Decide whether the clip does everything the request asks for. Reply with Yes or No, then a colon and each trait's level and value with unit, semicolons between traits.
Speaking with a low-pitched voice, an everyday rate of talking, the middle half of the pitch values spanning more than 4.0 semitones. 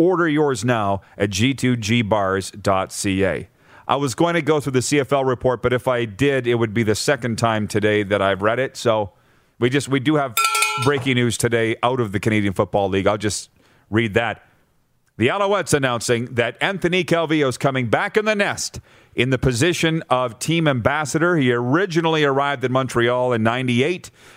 Yes: low, 125 Hz; average, 180 wpm; average, 4.4 semitones